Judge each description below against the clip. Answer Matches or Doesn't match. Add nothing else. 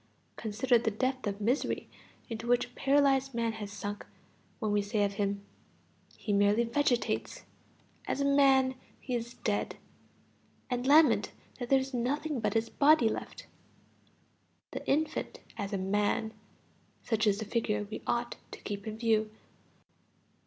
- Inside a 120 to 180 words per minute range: Matches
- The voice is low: Doesn't match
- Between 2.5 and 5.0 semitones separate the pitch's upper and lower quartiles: Matches